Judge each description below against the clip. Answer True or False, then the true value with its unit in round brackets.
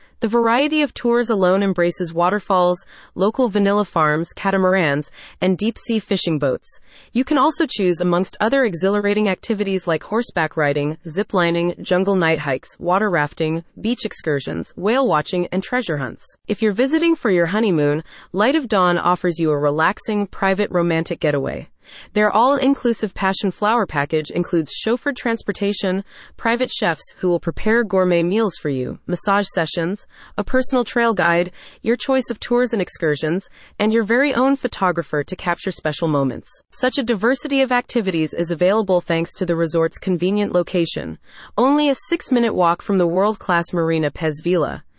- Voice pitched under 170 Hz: False (190 Hz)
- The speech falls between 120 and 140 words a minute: False (155 wpm)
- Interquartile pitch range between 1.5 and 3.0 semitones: False (5.1 semitones)